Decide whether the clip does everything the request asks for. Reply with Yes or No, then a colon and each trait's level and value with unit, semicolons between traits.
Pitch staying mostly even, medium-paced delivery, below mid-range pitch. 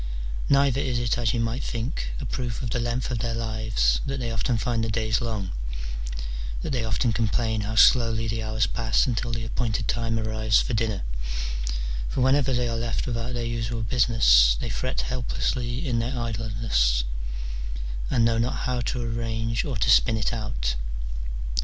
Yes: narrow, 1.7 semitones; average, 180 wpm; low, 115 Hz